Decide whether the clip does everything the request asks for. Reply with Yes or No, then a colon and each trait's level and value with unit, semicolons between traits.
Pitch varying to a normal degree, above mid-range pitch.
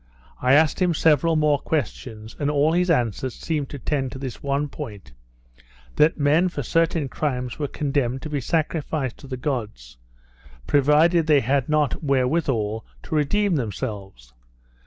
No: average, 3.7 semitones; medium, 140 Hz